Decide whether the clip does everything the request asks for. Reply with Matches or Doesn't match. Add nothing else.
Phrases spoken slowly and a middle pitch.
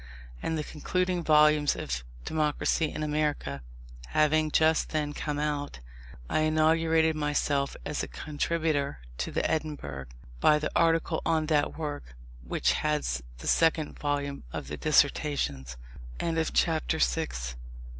Matches